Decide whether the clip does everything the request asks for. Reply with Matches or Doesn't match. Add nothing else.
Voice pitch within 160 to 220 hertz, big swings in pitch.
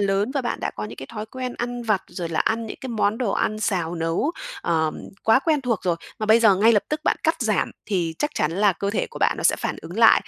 Doesn't match